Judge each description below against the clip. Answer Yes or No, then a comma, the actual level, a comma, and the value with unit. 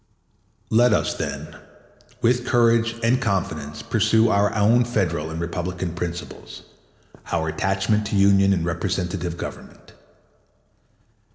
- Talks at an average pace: No, slow, 115 wpm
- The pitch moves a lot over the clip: No, average, 4.6 semitones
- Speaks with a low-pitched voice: Yes, low, 100 Hz